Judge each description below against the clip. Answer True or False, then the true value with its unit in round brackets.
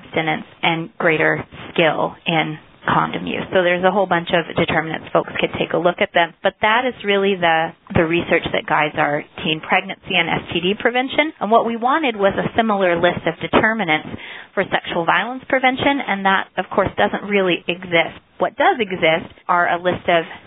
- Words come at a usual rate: True (185 wpm)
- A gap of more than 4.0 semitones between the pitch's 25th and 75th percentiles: False (3.7 semitones)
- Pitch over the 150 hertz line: True (185 Hz)